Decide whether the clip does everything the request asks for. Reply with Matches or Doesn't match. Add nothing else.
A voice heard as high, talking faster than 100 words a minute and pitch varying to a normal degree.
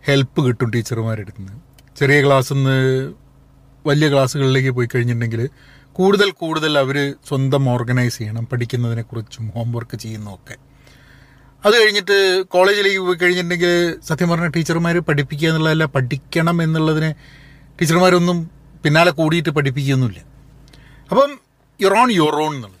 Doesn't match